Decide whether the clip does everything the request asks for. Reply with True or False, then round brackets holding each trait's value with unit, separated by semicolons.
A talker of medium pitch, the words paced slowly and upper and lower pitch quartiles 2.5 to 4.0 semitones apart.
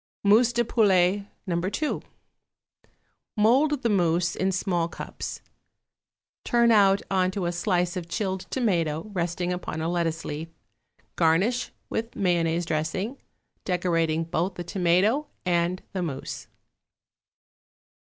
True (180 Hz; 120 wpm; 3.4 semitones)